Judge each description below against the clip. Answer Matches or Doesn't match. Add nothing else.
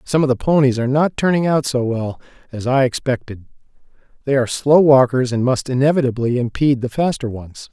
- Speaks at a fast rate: Doesn't match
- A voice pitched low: Matches